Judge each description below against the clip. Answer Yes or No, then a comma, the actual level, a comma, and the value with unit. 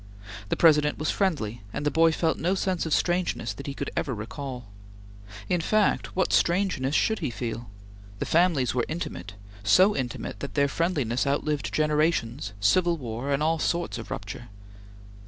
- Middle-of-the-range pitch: Yes, medium, 150 Hz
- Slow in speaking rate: No, average, 165 wpm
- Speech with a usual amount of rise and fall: No, wide, 5.8 semitones